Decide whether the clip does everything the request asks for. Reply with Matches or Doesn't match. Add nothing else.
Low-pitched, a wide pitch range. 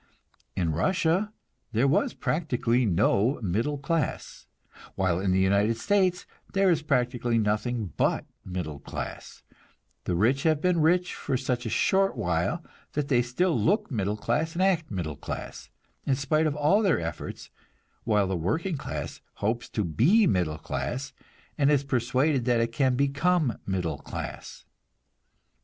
Matches